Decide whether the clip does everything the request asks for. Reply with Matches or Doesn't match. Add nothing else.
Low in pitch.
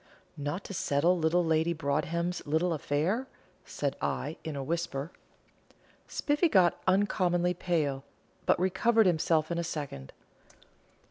Doesn't match